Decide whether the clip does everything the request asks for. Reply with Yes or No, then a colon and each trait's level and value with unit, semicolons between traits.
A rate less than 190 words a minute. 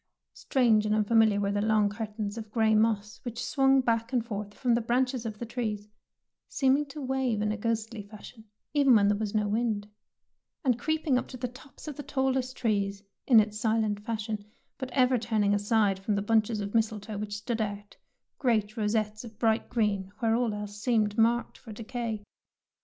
No: average, 195 wpm